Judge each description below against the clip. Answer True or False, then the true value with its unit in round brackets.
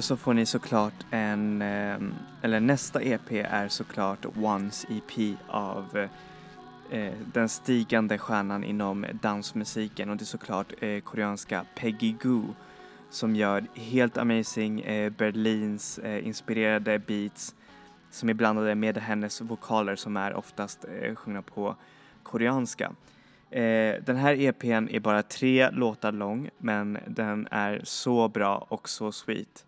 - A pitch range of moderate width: False (1.8 semitones)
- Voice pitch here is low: True (110 Hz)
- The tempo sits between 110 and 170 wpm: True (135 wpm)